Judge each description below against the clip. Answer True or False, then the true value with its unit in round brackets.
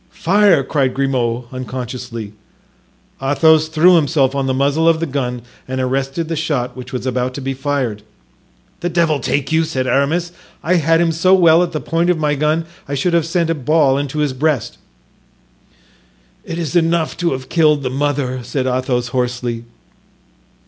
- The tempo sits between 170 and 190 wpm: True (175 wpm)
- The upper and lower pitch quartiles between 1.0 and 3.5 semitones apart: False (4.1 semitones)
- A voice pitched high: False (145 Hz)